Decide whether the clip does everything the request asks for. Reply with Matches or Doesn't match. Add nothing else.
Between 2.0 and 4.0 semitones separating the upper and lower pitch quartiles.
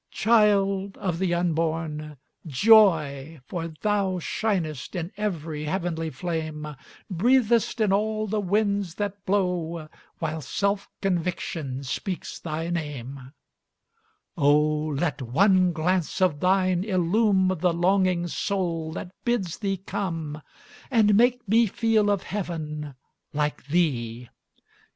Doesn't match